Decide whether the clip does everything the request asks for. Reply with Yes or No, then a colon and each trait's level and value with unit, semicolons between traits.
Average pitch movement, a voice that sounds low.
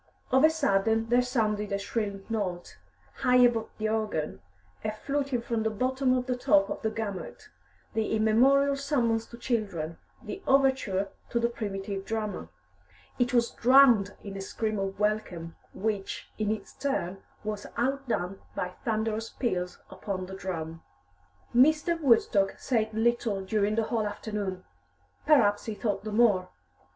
No: average, 3.5 semitones; high, 220 Hz